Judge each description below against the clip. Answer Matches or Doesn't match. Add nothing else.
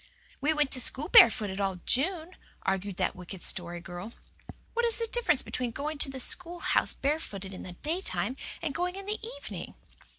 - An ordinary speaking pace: Matches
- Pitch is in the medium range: Doesn't match